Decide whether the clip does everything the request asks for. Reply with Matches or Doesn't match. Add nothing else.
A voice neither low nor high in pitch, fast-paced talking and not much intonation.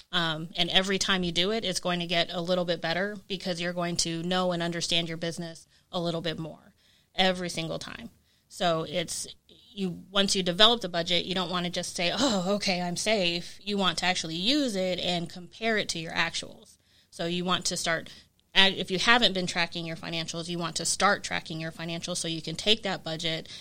Matches